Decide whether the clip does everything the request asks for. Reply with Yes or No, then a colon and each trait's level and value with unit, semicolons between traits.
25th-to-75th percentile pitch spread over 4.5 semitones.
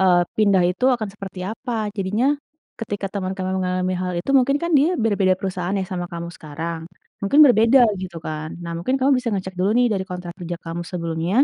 No: average, 3.7 semitones